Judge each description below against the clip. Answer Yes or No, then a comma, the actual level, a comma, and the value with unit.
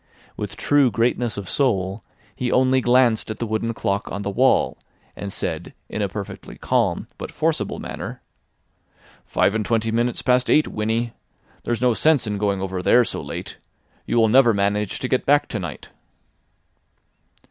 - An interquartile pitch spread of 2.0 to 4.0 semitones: Yes, average, 3.5 semitones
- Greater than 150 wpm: Yes, average, 170 wpm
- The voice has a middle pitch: No, low, 115 Hz